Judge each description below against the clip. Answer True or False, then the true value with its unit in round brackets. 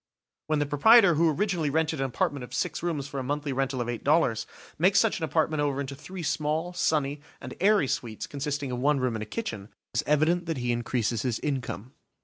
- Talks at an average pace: False (220 wpm)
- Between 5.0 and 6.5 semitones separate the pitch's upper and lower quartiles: False (3.9 semitones)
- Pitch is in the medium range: True (145 Hz)